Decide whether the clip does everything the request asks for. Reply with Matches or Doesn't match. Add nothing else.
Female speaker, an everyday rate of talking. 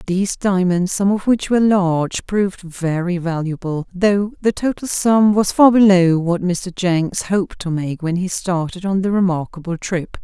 Matches